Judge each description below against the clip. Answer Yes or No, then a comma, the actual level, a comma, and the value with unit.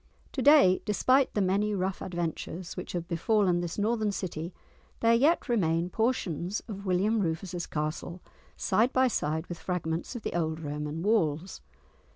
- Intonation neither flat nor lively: Yes, average, 4.6 semitones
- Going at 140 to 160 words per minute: Yes, average, 155 wpm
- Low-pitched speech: No, medium, 185 Hz